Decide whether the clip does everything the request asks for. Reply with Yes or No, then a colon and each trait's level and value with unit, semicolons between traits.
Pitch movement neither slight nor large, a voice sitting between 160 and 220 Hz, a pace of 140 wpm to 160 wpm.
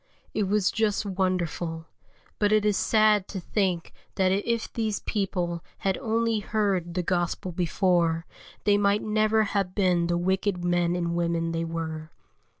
Yes: average, 3.3 semitones; medium, 185 Hz; average, 150 wpm